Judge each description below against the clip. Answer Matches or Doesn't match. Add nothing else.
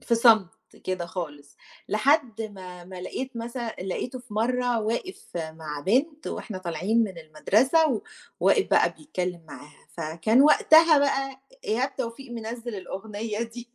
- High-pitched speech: Matches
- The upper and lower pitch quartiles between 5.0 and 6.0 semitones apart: Matches